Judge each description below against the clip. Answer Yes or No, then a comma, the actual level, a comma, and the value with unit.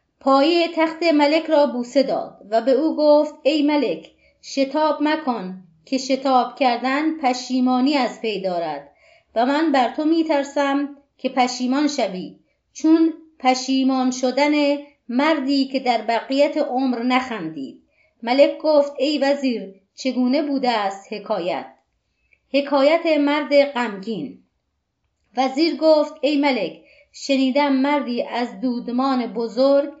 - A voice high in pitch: Yes, very high, 275 Hz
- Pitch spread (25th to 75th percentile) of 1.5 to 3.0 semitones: Yes, average, 2.7 semitones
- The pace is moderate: Yes, average, 120 wpm